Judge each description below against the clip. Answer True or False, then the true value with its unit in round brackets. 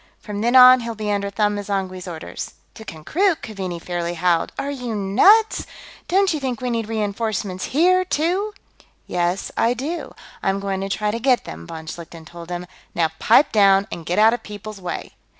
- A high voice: True (210 Hz)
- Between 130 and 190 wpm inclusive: True (185 wpm)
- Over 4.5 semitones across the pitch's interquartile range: True (5.4 semitones)